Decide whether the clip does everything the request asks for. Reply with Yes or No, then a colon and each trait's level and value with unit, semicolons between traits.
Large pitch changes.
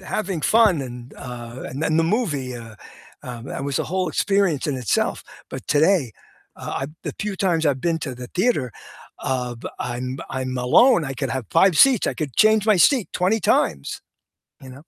Yes: wide, 6.9 semitones